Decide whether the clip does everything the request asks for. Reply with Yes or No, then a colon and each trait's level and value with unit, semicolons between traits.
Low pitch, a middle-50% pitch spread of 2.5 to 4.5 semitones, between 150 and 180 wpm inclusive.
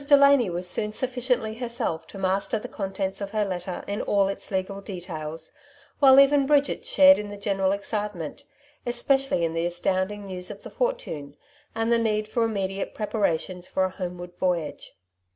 No: high, 200 Hz; average, 4.2 semitones; average, 170 wpm